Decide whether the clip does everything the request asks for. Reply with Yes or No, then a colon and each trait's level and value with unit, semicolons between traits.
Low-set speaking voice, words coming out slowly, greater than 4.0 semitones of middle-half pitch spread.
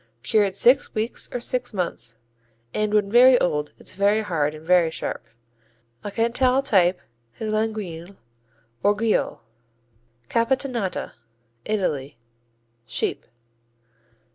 No: high, 205 Hz; slow, 110 wpm; average, 4.6 semitones